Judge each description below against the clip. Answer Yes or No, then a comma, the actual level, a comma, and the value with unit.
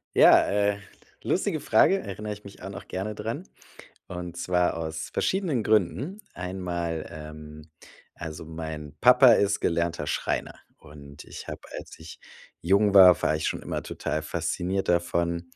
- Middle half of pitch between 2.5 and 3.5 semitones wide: No, average, 4.1 semitones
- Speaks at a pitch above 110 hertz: No, very low, 90 Hz